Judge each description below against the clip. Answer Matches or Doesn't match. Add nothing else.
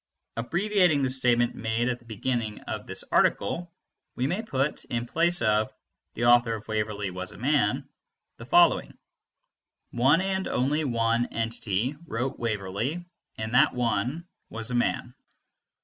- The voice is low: Matches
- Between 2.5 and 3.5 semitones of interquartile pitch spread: Doesn't match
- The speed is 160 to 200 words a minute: Doesn't match